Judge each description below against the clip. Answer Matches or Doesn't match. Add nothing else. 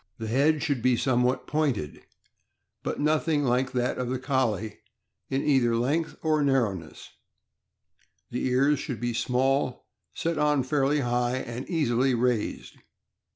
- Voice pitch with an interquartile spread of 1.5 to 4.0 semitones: Matches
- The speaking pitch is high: Doesn't match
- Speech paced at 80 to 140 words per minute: Matches